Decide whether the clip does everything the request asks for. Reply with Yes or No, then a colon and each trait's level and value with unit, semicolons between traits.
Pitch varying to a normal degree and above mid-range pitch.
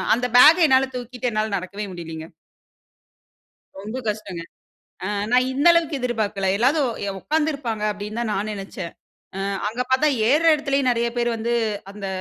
Yes: average, 4.4 semitones; high, 235 Hz